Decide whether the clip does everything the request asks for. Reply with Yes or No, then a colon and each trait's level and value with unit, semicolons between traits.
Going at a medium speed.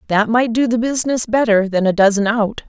No: fast, 225 wpm